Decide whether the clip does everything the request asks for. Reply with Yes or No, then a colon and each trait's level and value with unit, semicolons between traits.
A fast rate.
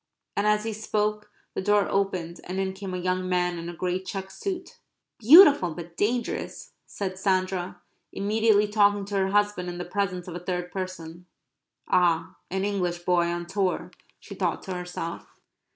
No: average, 170 wpm